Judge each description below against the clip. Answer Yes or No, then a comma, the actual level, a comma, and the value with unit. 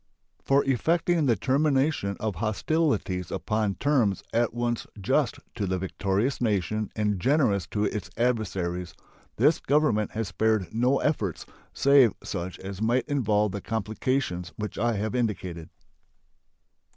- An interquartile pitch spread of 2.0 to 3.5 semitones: No, average, 4.8 semitones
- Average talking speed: No, slow, 130 wpm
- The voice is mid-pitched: No, low, 110 Hz